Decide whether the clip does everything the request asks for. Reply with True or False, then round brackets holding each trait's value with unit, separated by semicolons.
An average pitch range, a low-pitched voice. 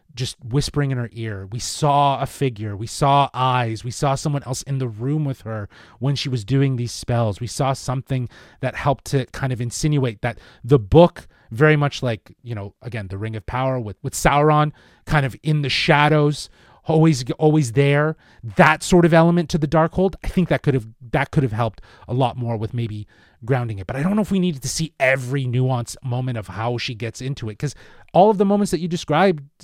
True (4.0 semitones; 130 Hz)